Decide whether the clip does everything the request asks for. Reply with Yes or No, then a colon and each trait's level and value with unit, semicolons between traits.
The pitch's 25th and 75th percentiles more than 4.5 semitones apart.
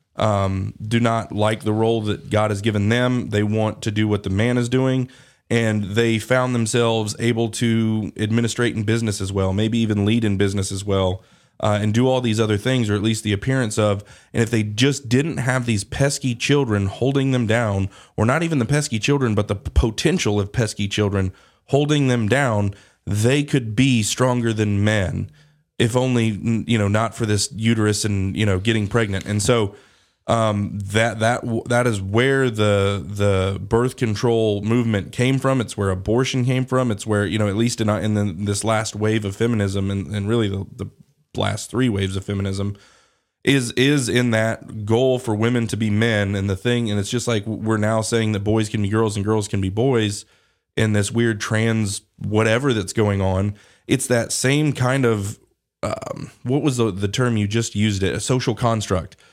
No: average, 2.8 semitones